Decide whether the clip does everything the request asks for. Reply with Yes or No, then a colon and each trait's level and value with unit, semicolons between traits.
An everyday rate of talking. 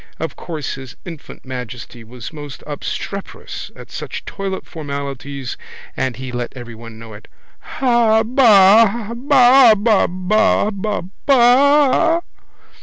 No: slow, 100 wpm